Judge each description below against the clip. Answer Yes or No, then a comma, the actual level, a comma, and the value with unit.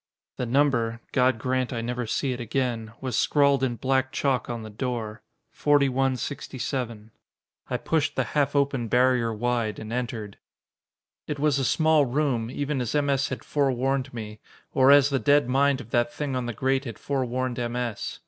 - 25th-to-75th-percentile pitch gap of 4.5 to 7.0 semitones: No, average, 2.7 semitones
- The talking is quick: No, average, 175 wpm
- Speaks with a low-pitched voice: Yes, low, 130 Hz